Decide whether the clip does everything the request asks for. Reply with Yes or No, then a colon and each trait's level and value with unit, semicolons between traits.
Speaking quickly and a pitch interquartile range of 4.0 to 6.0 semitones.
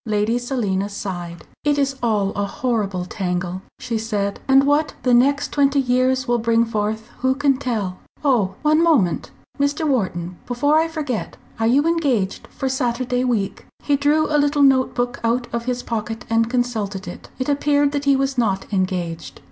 No: average, 175 wpm; average, 5.1 semitones